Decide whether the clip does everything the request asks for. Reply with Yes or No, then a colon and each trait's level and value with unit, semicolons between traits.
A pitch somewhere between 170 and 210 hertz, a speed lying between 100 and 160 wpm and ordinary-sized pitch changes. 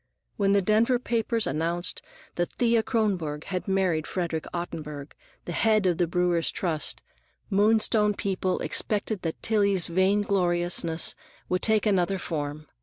Yes: medium, 185 Hz; slow, 135 wpm; average, 3.6 semitones